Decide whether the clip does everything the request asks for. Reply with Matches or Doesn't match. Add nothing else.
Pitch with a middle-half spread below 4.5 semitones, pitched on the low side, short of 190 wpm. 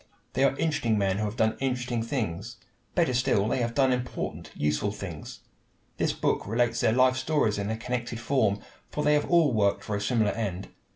Doesn't match